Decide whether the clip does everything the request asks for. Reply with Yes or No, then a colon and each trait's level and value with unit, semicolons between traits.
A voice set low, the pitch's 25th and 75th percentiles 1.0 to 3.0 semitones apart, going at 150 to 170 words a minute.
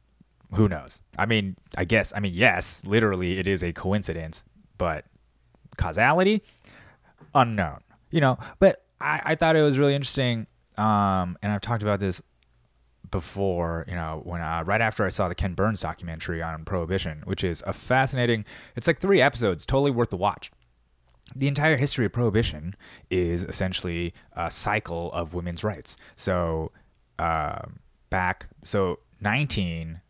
No: low, 100 Hz; average, 5.2 semitones; average, 155 wpm